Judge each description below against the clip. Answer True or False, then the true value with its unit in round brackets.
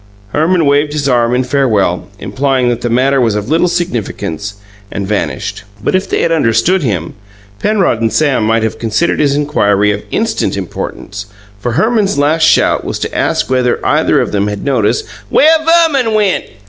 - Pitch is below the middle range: True (130 Hz)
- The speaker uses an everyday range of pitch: False (7.2 semitones)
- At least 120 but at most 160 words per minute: False (175 wpm)